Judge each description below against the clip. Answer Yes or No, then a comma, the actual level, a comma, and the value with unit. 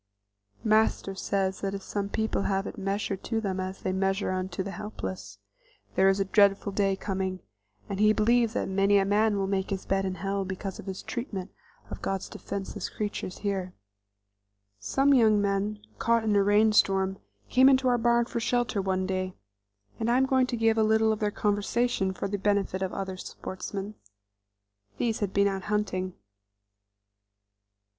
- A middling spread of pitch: No, narrow, 2.2 semitones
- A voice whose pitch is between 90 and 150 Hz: No, high, 200 Hz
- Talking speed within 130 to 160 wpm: No, average, 180 wpm